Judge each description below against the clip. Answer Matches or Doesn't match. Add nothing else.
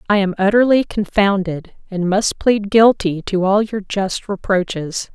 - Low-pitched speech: Doesn't match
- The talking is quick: Doesn't match